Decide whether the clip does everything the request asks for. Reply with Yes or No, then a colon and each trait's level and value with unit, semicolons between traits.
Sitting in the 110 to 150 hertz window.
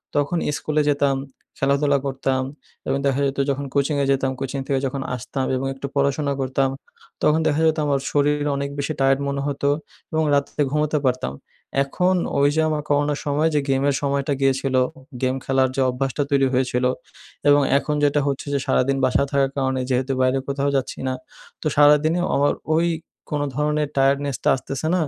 Yes: medium, 140 Hz